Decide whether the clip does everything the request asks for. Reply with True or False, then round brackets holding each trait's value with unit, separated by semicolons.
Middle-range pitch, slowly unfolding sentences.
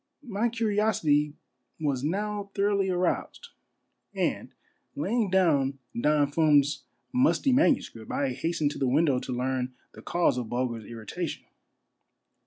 True (155 Hz; 120 wpm)